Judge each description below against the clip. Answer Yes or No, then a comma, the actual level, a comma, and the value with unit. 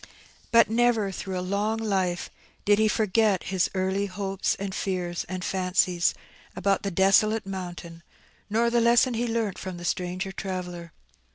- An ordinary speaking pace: Yes, average, 155 wpm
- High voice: Yes, high, 195 Hz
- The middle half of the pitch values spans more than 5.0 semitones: No, average, 2.9 semitones